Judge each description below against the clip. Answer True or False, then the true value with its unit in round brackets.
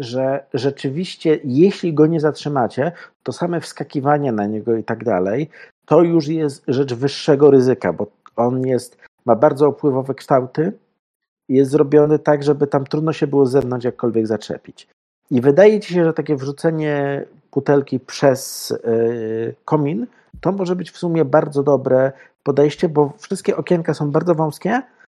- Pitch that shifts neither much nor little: True (3.2 semitones)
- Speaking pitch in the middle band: True (145 Hz)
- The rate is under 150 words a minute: False (155 wpm)